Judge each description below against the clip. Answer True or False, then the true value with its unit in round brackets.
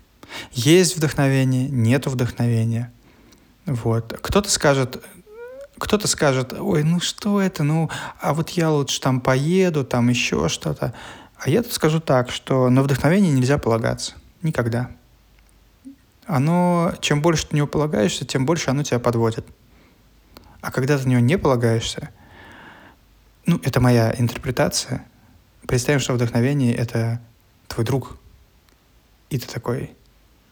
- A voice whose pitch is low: True (130 Hz)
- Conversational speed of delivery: True (130 wpm)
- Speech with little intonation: False (4.6 semitones)